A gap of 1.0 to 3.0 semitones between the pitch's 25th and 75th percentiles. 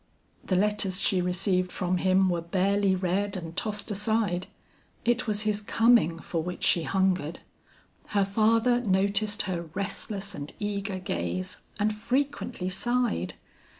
Yes: average, 2.7 semitones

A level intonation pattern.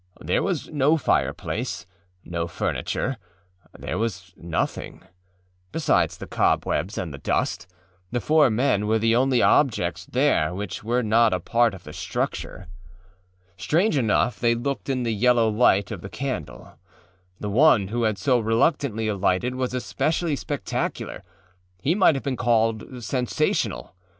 No: average, 4.2 semitones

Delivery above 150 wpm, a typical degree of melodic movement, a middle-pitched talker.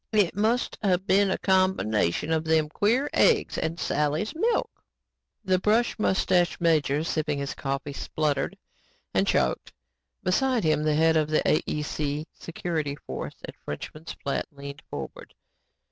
No: average, 140 wpm; average, 4.2 semitones; medium, 160 Hz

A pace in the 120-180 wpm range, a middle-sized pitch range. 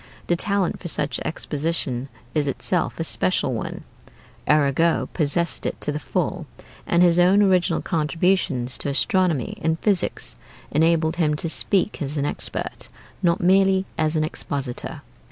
Yes: average, 145 wpm; average, 3.3 semitones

